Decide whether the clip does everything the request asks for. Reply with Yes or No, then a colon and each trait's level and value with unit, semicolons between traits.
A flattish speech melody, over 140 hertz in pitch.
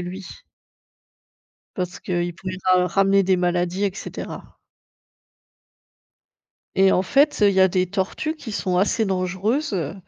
Yes: narrow, 1.7 semitones; high, 190 Hz